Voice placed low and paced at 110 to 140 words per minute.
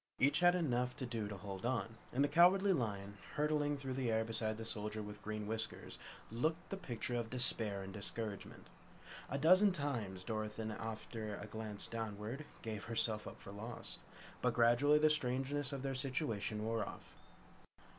No: low, 115 Hz; average, 170 wpm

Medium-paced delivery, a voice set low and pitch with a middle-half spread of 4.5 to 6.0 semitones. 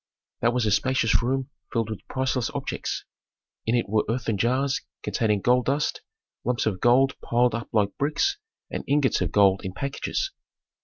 No: average, 165 wpm; low, 120 Hz; average, 3.5 semitones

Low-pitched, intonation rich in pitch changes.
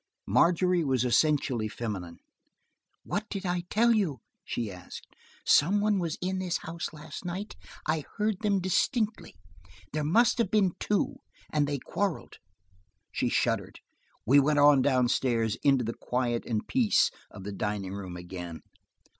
No: medium, 150 Hz; wide, 8.3 semitones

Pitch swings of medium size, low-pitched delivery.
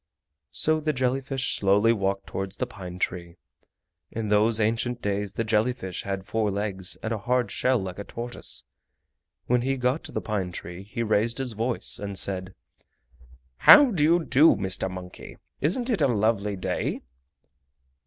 Yes: average, 4.4 semitones; low, 110 Hz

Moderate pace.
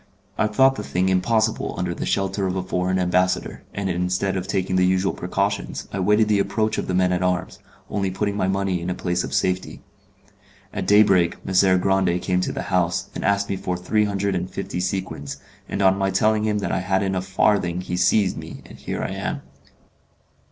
No: fast, 210 wpm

